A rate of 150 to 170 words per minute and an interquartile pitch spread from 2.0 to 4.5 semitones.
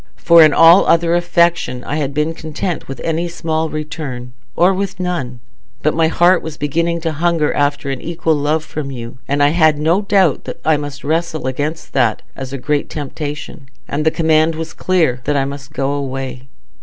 No: average, 195 wpm; average, 2.9 semitones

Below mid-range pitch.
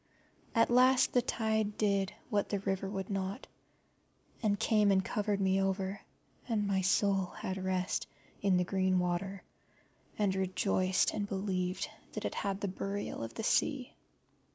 No: high, 195 Hz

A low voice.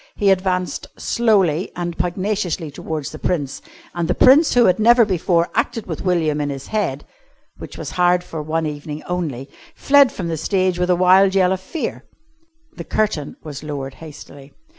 No: medium, 180 Hz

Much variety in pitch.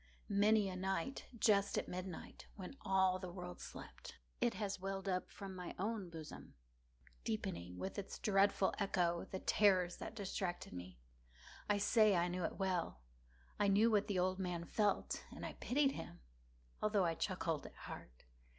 No: narrow, 2.4 semitones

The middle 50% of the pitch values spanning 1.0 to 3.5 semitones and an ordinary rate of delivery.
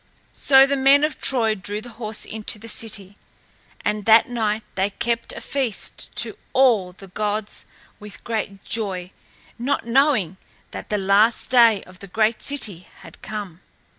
Yes: average, 3.1 semitones; average, 160 wpm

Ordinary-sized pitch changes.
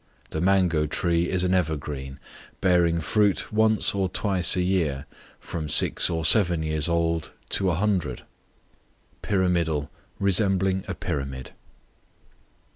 Yes: average, 3.4 semitones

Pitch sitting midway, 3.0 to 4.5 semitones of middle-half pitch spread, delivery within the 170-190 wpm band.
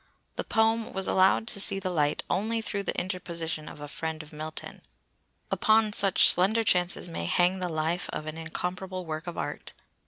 Yes: medium, 180 Hz; average, 3.5 semitones; average, 185 wpm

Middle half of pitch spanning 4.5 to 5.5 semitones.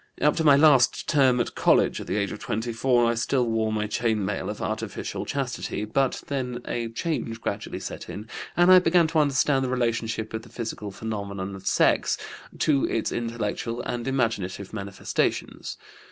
No: average, 3.7 semitones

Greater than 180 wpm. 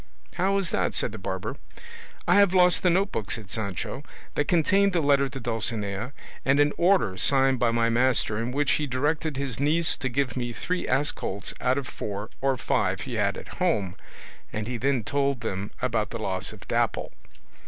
Yes: average, 195 wpm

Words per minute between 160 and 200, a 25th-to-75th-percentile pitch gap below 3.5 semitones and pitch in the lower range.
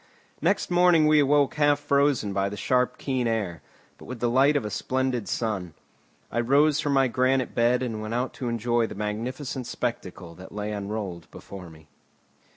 No: average, 180 wpm; average, 4.5 semitones; low, 120 Hz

